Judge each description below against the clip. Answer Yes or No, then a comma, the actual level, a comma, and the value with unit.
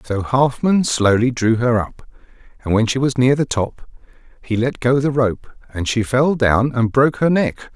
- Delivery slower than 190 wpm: No, average, 200 wpm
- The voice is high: No, low, 125 Hz